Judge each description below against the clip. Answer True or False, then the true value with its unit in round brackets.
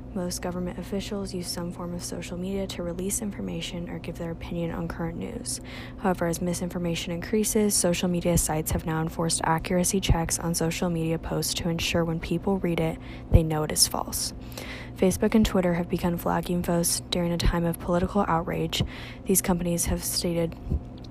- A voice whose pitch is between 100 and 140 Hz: False (175 Hz)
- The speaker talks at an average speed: True (180 wpm)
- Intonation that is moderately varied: False (1.7 semitones)